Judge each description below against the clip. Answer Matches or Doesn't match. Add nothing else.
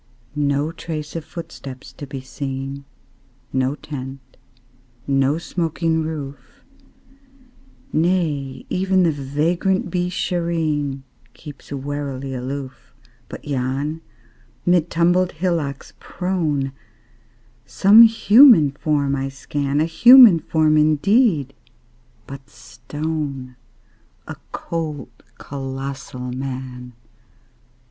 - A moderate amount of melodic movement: Matches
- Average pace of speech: Doesn't match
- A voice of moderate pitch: Matches